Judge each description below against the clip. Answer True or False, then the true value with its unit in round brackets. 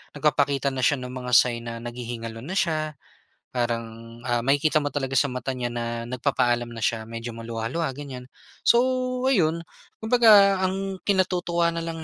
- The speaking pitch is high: False (130 Hz)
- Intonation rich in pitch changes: True (6.0 semitones)